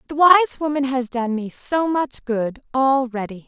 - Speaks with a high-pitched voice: Yes, very high, 265 Hz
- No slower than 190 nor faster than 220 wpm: No, average, 175 wpm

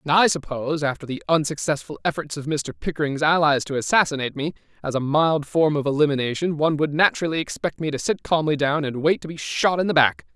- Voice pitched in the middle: Yes, medium, 145 Hz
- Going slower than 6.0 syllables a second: No, 6.3 syllables/s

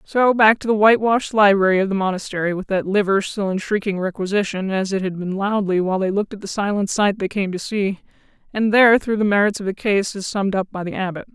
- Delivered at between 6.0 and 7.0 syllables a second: Yes, 6.3 syllables/s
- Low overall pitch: No, high, 200 Hz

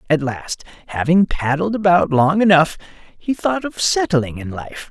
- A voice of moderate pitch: Yes, medium, 165 Hz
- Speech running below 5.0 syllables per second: Yes, 4.4 syllables/s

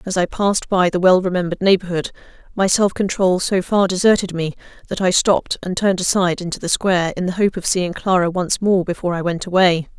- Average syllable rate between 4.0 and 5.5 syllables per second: No, 6.1 syllables/s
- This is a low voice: No, medium, 185 Hz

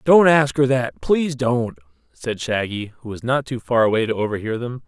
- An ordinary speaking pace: No, fast, 210 wpm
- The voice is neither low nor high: No, low, 120 Hz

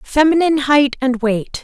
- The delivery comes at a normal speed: Yes, average, 145 wpm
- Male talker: No, female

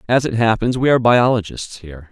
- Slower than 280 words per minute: Yes, average, 200 wpm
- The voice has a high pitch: No, low, 115 Hz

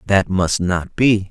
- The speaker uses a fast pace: No, average, 185 wpm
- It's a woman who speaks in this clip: No, male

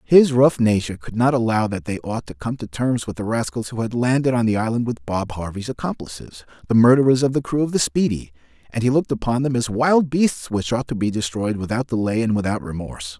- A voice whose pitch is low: Yes, low, 115 Hz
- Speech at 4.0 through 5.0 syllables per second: No, 5.9 syllables/s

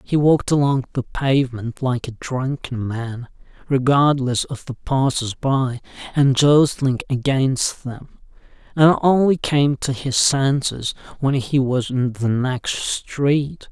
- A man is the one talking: Yes, male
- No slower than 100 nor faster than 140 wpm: Yes, slow, 135 wpm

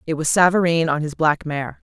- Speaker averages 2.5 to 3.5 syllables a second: No, 5.3 syllables/s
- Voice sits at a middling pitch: Yes, medium, 160 Hz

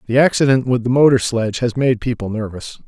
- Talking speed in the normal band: No, fast, 210 wpm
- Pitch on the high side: No, low, 120 Hz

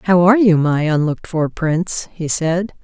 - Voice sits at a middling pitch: Yes, medium, 170 Hz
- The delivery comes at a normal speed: Yes, average, 190 wpm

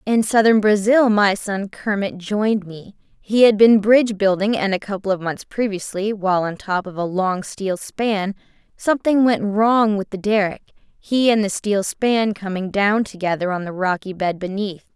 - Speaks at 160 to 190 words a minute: Yes, average, 185 wpm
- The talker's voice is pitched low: No, high, 205 Hz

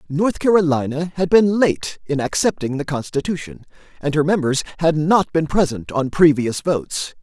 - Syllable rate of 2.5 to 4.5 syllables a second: No, 4.8 syllables/s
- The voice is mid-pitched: Yes, medium, 155 Hz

